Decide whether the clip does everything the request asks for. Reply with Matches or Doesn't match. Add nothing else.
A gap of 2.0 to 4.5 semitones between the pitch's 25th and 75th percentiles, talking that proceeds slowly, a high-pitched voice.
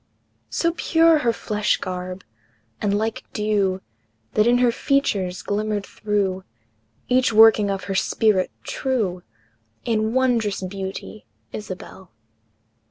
Matches